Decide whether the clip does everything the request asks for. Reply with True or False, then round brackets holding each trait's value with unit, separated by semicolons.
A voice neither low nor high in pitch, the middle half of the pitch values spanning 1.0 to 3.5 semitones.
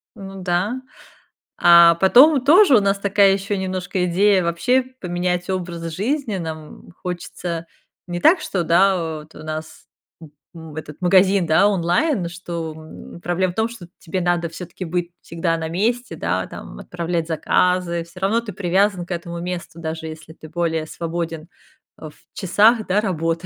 True (175 Hz; 2.8 semitones)